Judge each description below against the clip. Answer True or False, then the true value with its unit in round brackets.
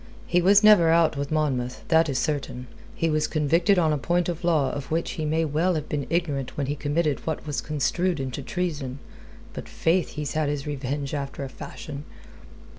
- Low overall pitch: False (150 Hz)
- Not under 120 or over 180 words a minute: False (195 wpm)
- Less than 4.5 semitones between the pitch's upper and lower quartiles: True (3.0 semitones)